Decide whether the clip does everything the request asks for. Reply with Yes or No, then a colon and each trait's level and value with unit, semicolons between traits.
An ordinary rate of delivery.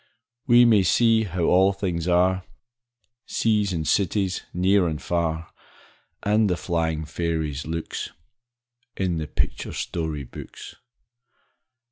No: slow, 115 wpm